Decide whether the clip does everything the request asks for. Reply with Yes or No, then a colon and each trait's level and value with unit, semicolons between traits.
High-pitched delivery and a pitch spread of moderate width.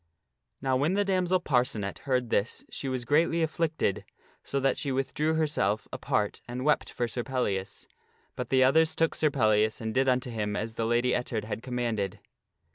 No: low, 130 Hz; average, 4.9 semitones